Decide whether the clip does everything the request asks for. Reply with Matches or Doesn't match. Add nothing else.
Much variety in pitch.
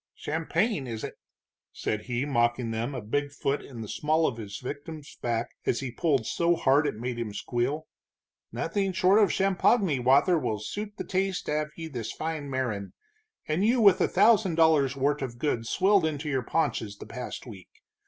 Matches